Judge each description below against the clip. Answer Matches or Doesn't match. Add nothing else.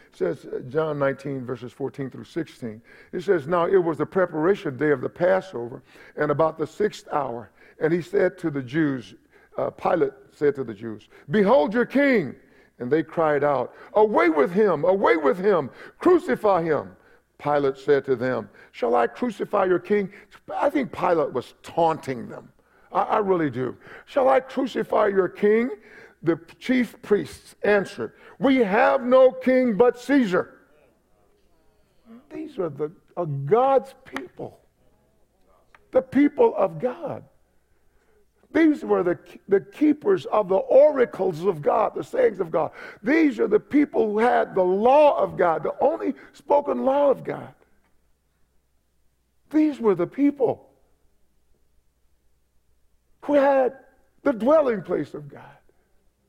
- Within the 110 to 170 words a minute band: Matches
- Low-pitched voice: Doesn't match